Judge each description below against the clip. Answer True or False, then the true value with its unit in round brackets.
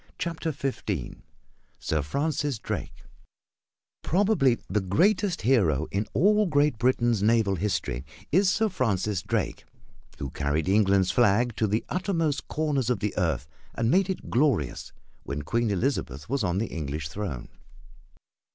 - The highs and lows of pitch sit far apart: True (8.2 semitones)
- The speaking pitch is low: True (115 Hz)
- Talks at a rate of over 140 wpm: False (135 wpm)